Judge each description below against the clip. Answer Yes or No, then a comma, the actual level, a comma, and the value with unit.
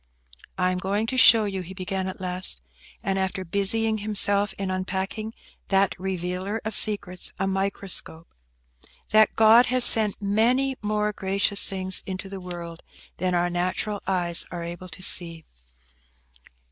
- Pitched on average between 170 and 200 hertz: Yes, high, 190 Hz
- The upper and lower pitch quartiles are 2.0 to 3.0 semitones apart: Yes, narrow, 2.5 semitones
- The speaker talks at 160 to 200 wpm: No, average, 145 wpm